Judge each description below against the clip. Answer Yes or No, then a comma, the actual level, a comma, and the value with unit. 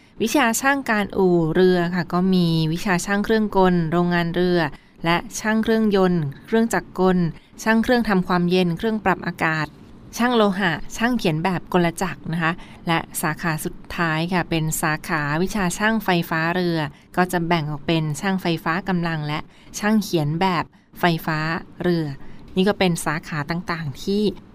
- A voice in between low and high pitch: Yes, medium, 175 Hz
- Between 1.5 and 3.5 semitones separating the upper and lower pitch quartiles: Yes, average, 2.9 semitones